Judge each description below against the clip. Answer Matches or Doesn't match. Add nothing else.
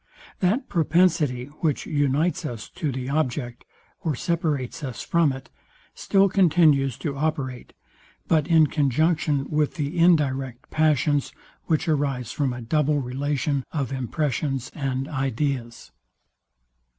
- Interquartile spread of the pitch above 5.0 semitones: Doesn't match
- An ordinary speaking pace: Doesn't match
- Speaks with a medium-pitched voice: Matches